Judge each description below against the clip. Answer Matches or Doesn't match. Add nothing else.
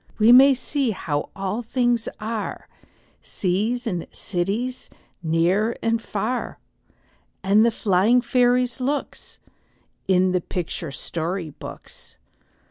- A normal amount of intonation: Matches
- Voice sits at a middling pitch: Doesn't match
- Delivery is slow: Matches